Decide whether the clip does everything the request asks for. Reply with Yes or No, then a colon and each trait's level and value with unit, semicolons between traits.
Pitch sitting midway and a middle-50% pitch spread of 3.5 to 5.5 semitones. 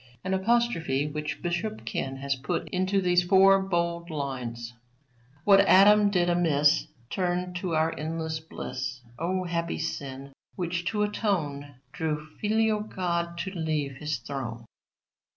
Yes: medium, 170 Hz; average, 4.5 semitones